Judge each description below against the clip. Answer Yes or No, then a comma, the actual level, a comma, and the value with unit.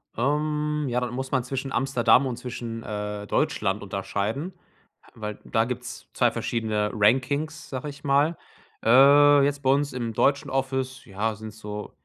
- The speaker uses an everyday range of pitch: Yes, average, 4.2 semitones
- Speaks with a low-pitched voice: Yes, low, 125 Hz